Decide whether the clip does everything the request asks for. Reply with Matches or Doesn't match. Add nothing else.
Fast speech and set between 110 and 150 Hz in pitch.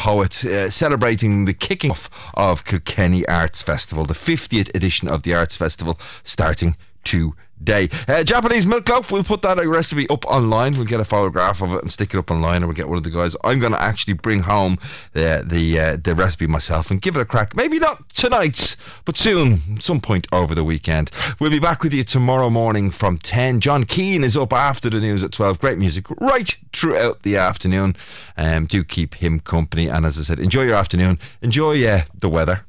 Doesn't match